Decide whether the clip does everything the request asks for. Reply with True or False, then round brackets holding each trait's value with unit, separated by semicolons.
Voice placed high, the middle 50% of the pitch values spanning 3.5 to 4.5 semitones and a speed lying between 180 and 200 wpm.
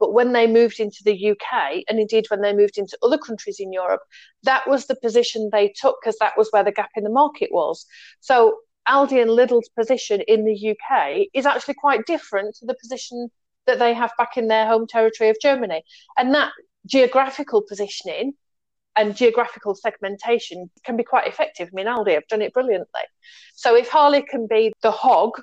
True (235 Hz; 4.0 semitones; 195 wpm)